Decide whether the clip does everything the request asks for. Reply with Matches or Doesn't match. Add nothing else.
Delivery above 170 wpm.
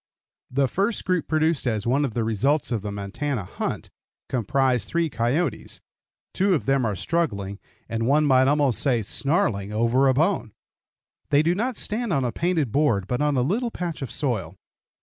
Matches